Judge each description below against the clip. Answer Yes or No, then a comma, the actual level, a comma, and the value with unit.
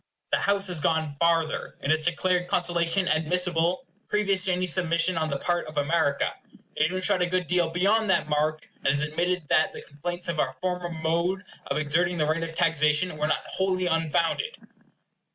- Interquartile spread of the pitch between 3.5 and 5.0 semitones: No, narrow, 2.5 semitones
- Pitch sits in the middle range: Yes, medium, 170 Hz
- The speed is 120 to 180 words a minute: No, average, 190 wpm